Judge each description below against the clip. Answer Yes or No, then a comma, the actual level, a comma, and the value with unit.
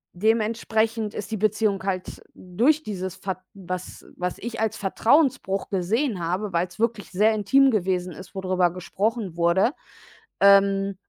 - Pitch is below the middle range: No, high, 200 Hz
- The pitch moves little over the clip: No, average, 3.2 semitones